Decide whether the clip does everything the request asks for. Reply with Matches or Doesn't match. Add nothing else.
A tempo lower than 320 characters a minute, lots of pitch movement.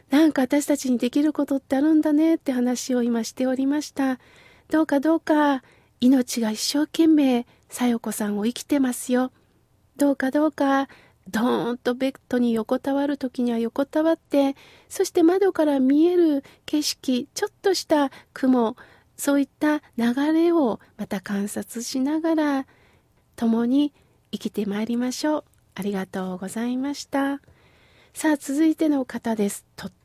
Doesn't match